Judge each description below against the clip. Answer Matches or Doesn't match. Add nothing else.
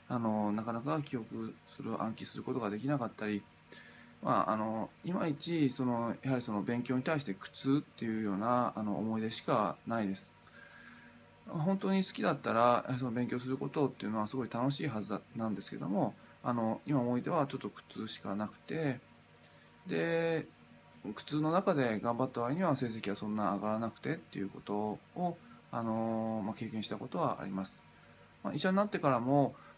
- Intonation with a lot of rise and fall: Doesn't match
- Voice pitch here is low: Matches